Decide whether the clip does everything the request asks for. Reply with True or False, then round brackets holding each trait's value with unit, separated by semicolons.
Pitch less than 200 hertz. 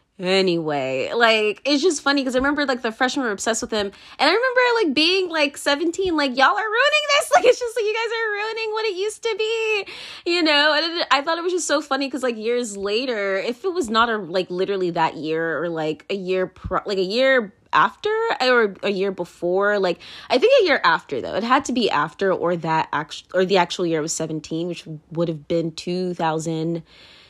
False (235 Hz)